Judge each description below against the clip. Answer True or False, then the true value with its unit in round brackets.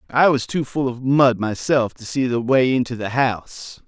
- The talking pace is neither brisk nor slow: False (215 wpm)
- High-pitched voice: False (125 Hz)